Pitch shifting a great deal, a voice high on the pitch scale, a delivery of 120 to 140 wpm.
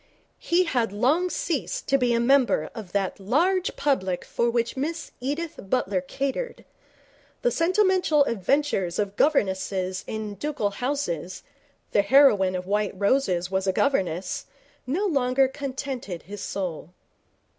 Yes: wide, 7.0 semitones; high, 240 Hz; slow, 135 wpm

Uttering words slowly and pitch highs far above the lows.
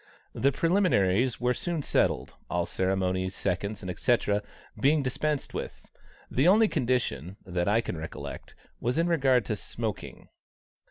Yes: slow, 130 wpm; wide, 7.7 semitones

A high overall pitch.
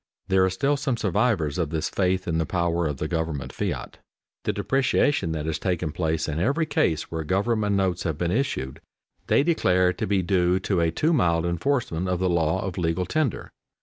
No: very low, 90 Hz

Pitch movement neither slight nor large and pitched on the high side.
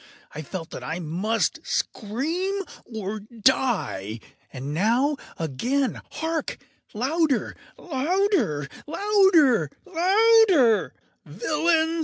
No: wide, 9.0 semitones; very high, 260 Hz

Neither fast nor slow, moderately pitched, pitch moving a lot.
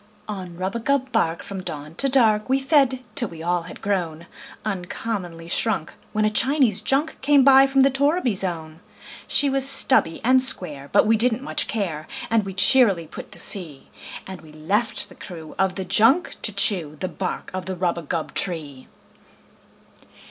No: average, 170 wpm; high, 200 Hz; wide, 7.2 semitones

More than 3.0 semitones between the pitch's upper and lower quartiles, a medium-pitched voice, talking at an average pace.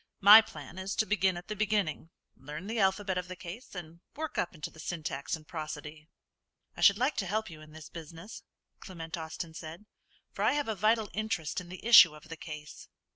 No: average, 4.9 semitones; medium, 175 Hz; fast, 210 wpm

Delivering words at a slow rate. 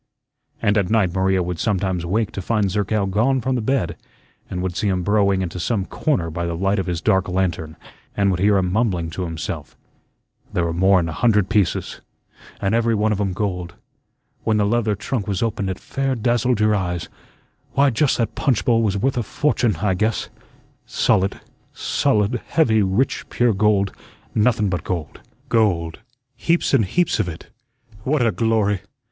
No: average, 180 wpm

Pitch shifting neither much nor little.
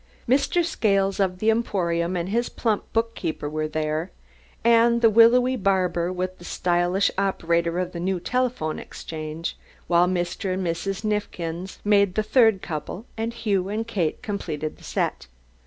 Yes: average, 4.5 semitones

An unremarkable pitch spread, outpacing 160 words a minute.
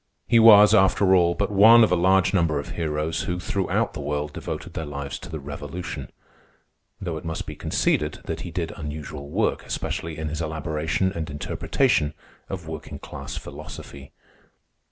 Yes: average, 3.9 semitones; average, 170 wpm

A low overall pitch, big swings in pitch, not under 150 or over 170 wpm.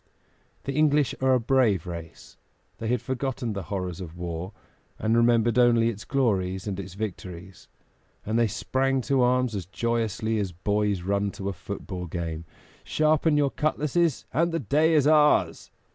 Yes: low, 115 Hz; wide, 5.9 semitones; average, 160 wpm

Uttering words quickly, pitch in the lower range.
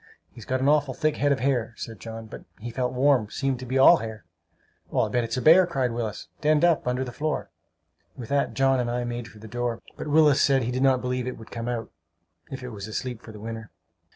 Yes: fast, 245 wpm; low, 125 Hz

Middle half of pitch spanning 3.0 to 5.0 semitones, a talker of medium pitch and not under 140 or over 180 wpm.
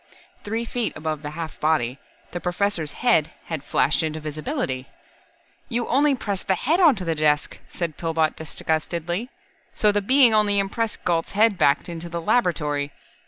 No: wide, 5.5 semitones; medium, 170 Hz; average, 160 wpm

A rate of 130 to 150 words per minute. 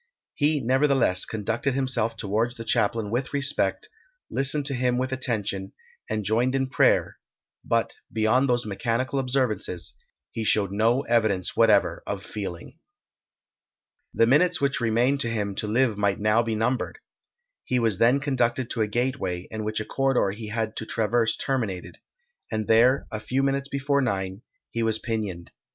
No: average, 160 wpm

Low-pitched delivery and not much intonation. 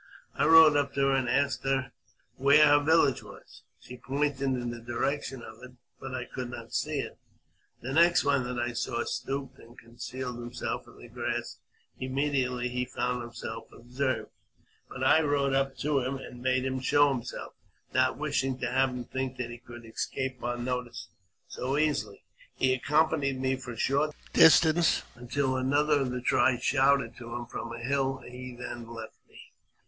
Yes: low, 130 Hz; narrow, 2.3 semitones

